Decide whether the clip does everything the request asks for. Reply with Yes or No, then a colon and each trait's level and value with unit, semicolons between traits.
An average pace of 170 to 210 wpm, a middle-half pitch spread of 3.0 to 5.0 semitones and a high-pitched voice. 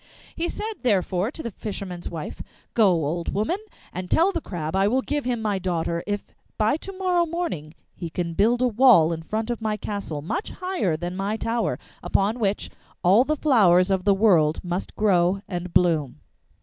No: average, 190 wpm; wide, 5.5 semitones; high, 200 Hz